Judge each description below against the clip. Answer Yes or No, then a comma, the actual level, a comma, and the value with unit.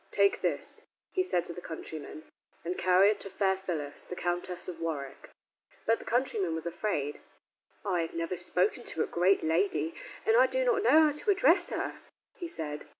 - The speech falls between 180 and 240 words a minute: Yes, average, 190 wpm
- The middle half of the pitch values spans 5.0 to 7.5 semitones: Yes, average, 5.3 semitones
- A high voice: No, medium, 180 Hz